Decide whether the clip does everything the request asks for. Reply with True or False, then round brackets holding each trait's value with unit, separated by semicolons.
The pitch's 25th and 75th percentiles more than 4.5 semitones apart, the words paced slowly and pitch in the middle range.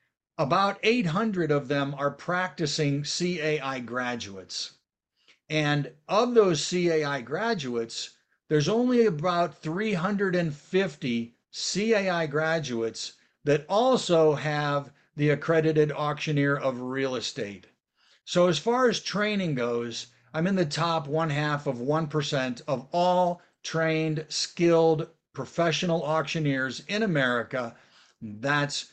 False (4.0 semitones; 105 wpm; 155 Hz)